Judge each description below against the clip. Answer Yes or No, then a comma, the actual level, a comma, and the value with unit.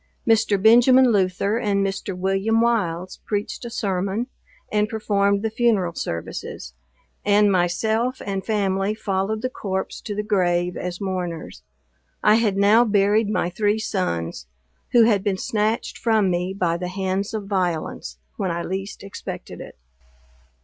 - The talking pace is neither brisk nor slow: Yes, average, 145 wpm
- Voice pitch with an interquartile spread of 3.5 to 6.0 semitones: No, average, 2.8 semitones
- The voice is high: Yes, high, 200 Hz